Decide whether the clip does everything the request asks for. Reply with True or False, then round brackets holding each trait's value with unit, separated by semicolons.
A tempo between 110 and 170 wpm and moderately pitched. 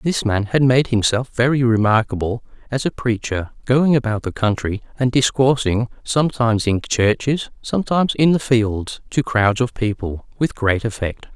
False (160 wpm; 120 Hz)